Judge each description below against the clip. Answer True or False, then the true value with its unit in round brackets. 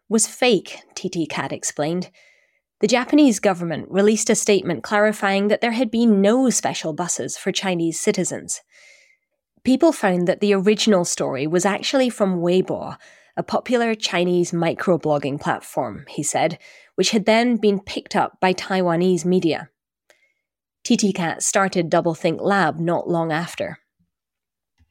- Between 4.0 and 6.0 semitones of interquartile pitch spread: True (4.3 semitones)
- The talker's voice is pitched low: False (185 Hz)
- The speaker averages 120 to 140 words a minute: True (135 wpm)